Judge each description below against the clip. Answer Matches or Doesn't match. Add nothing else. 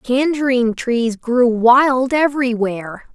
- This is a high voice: Matches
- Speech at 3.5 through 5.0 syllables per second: Matches